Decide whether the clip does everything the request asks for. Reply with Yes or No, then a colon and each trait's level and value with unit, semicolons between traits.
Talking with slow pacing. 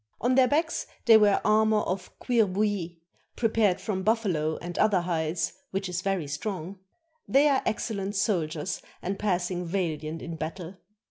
No: average, 150 wpm